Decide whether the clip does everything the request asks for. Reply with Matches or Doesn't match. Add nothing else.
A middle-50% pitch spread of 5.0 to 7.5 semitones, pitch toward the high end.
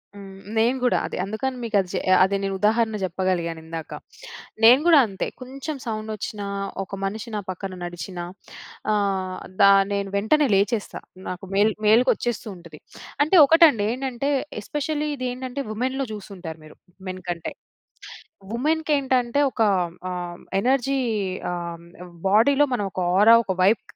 Matches